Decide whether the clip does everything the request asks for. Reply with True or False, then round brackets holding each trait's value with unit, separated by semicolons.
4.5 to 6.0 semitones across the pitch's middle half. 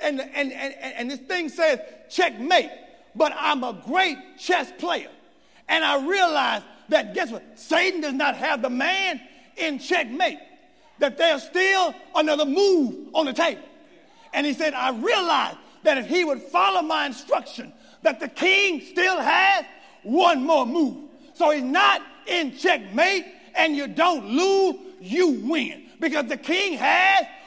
False (3.7 semitones)